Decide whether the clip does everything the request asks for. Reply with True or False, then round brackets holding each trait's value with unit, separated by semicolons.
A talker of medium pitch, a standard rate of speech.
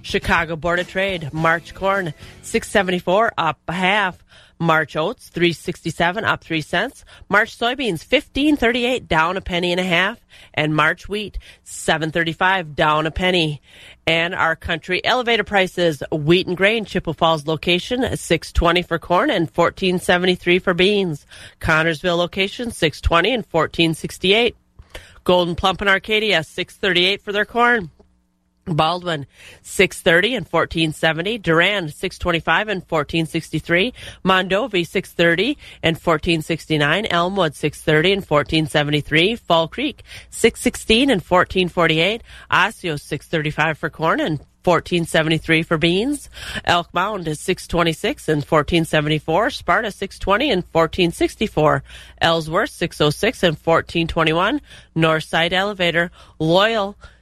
False (175 Hz; 115 wpm)